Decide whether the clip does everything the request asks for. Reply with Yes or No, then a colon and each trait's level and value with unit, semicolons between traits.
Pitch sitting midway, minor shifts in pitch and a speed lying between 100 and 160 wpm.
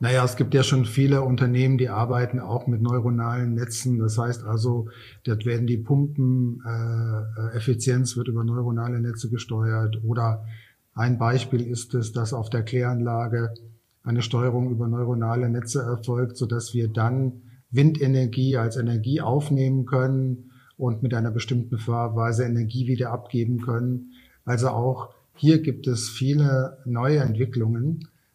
No: low, 120 Hz; narrow, 1.7 semitones; average, 140 wpm